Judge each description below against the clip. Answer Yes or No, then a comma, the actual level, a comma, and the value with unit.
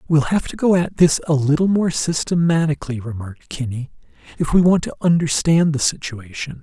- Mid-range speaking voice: Yes, medium, 155 Hz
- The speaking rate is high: No, average, 170 wpm